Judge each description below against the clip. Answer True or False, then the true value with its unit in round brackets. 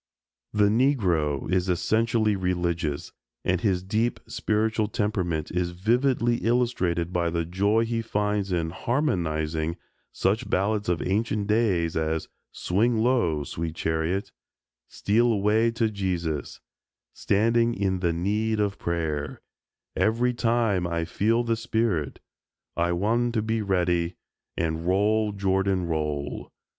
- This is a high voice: False (100 Hz)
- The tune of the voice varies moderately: True (4.6 semitones)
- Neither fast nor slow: False (125 wpm)